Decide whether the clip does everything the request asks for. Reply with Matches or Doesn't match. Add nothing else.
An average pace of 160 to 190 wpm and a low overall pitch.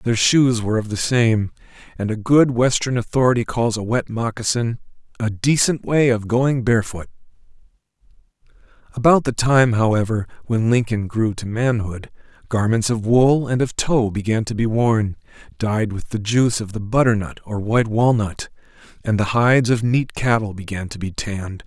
Matches